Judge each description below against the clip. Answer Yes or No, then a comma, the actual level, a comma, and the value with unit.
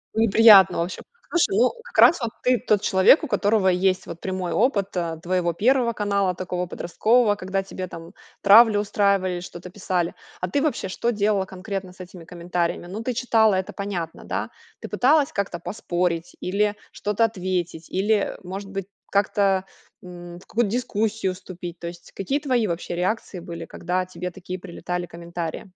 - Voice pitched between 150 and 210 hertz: Yes, high, 190 Hz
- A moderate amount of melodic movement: Yes, average, 3.0 semitones